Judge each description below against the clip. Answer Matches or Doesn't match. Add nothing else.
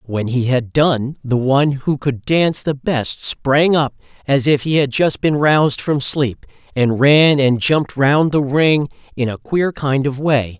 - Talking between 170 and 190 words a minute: Doesn't match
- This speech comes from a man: Matches